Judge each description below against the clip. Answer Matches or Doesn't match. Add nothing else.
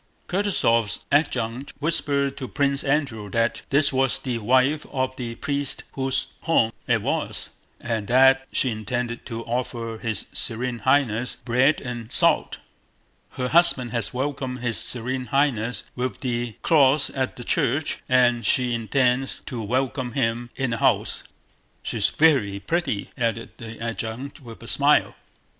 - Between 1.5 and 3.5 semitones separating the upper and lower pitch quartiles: Matches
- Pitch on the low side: Matches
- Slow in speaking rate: Doesn't match